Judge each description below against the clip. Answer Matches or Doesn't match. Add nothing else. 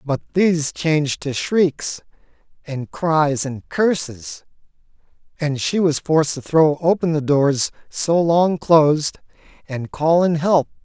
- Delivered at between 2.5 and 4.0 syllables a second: Matches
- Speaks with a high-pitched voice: Doesn't match